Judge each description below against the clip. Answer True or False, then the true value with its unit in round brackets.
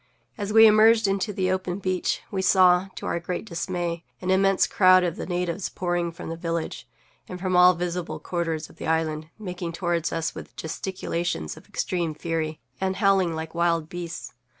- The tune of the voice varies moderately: False (2.1 semitones)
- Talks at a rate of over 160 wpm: True (180 wpm)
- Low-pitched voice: False (175 Hz)